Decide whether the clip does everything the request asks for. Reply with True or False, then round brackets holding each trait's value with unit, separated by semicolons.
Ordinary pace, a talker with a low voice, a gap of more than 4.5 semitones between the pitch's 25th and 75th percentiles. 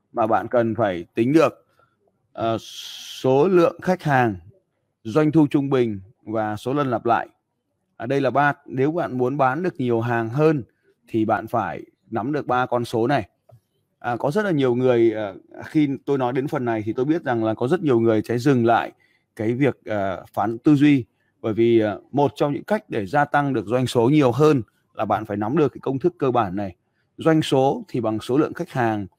False (220 wpm; 125 Hz; 4.1 semitones)